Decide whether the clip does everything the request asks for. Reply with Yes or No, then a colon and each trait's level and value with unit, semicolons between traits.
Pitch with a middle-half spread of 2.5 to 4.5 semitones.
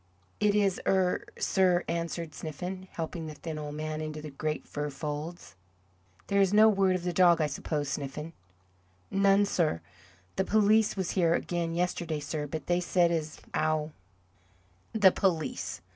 Yes: average, 3.6 semitones